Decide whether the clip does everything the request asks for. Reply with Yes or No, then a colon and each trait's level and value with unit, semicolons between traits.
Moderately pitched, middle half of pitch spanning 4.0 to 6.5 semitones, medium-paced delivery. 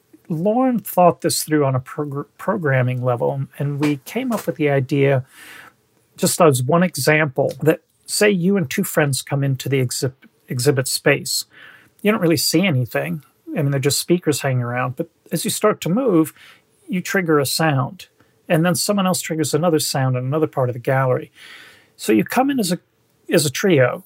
Yes: medium, 155 Hz; average, 4.6 semitones; average, 190 wpm